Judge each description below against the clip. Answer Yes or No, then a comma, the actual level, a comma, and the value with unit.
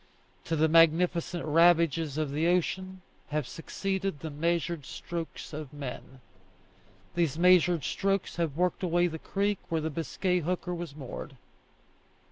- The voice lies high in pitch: No, medium, 165 Hz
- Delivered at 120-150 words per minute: Yes, slow, 135 wpm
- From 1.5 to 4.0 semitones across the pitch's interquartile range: Yes, narrow, 2.5 semitones